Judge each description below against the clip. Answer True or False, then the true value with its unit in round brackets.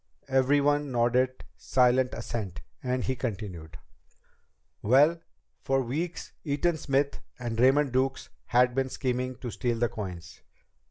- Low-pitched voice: True (130 Hz)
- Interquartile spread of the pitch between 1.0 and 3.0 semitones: True (2.4 semitones)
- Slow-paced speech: True (120 wpm)